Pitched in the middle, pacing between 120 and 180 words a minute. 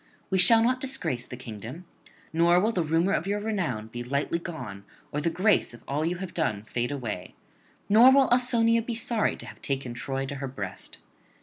No: medium, 165 Hz; average, 200 wpm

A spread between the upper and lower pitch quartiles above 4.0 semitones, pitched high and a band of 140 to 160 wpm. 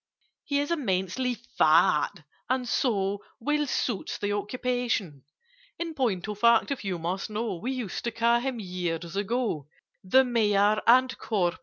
Yes: average, 4.9 semitones; high, 215 Hz; average, 150 wpm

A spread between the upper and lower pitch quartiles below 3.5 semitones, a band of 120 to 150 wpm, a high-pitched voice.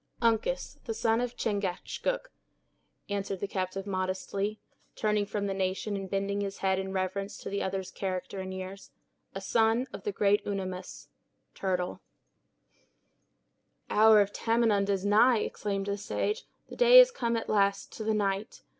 No: narrow, 2.4 semitones; average, 160 wpm; high, 200 Hz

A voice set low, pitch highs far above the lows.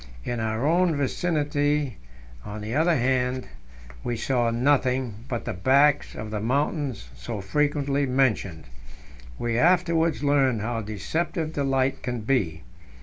No: low, 130 Hz; average, 4.4 semitones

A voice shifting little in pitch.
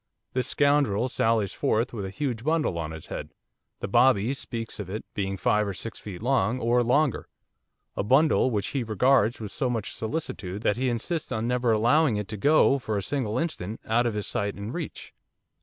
No: average, 4.1 semitones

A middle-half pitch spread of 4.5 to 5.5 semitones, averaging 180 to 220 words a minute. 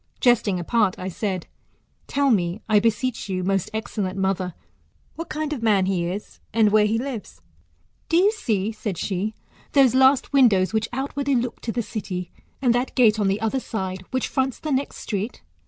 Yes: average, 5.0 semitones; average, 185 wpm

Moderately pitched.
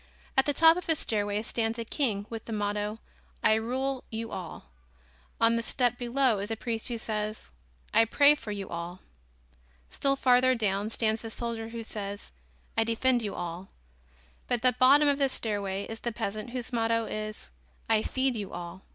No: high, 225 Hz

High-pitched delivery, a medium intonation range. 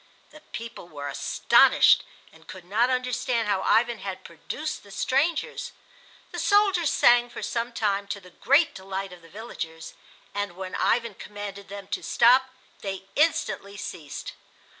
Yes: high, 205 Hz; average, 4.4 semitones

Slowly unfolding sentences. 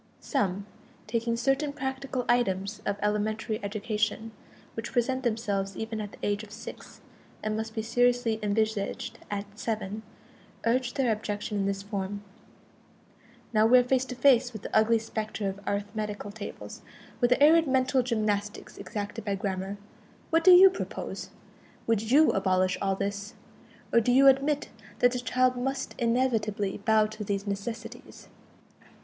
No: average, 150 wpm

